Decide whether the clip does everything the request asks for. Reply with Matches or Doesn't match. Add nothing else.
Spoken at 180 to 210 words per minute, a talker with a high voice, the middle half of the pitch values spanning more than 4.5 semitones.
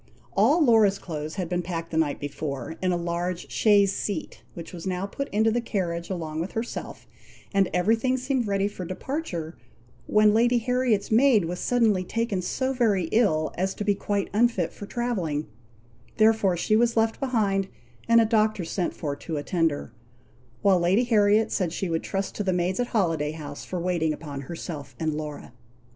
Matches